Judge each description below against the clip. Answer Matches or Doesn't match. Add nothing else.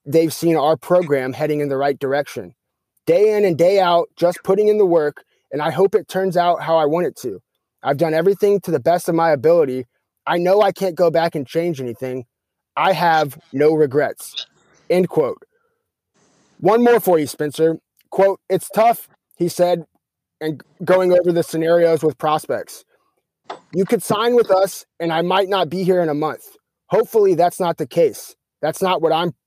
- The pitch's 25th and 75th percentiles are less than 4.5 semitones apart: Matches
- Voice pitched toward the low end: Doesn't match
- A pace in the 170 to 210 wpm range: Matches